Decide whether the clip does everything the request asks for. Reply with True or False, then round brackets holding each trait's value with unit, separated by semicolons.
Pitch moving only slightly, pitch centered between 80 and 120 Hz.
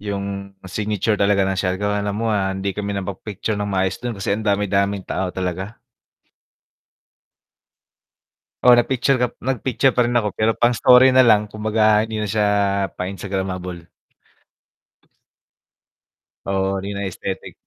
True (2.1 semitones; 100 Hz)